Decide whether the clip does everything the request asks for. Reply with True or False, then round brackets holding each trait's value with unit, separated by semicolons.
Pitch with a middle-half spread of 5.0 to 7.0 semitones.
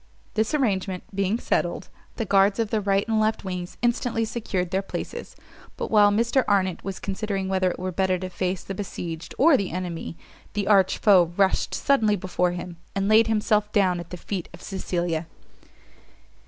False (2.8 semitones)